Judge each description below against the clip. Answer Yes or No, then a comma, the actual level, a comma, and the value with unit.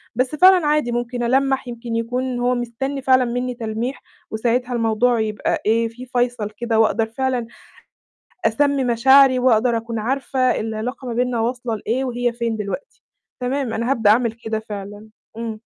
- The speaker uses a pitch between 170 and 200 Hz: No, high, 240 Hz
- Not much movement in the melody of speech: Yes, narrow, 2.2 semitones